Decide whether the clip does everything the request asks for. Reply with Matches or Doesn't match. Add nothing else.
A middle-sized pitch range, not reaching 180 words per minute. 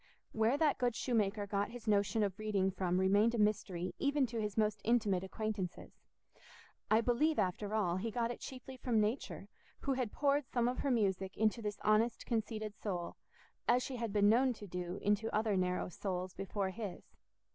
Doesn't match